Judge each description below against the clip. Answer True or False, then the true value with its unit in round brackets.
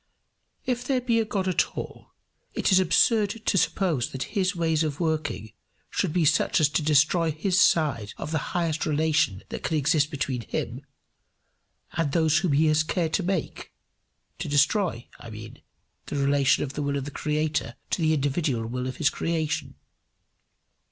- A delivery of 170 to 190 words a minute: True (175 wpm)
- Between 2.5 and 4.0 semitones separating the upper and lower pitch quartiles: True (3.6 semitones)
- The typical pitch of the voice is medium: True (155 Hz)